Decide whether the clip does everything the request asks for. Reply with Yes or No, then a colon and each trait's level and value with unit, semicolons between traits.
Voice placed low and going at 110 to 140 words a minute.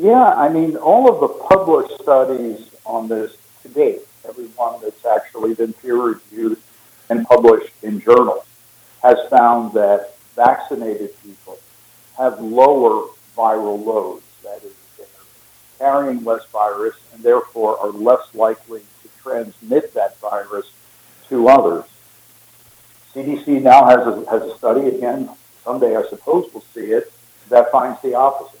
Yes: low, 130 Hz; slow, 135 wpm